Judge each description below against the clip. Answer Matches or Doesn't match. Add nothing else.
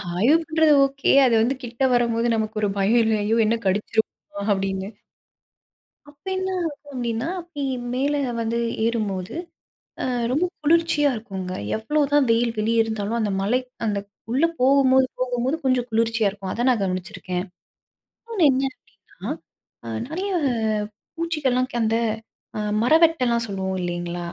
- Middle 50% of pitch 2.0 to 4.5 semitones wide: Doesn't match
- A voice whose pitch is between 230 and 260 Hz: Matches